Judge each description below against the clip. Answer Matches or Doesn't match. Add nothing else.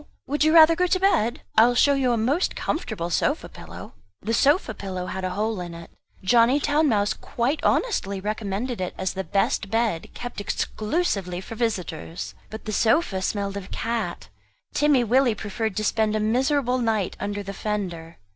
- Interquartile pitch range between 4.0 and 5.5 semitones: Matches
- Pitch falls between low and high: Doesn't match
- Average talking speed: Matches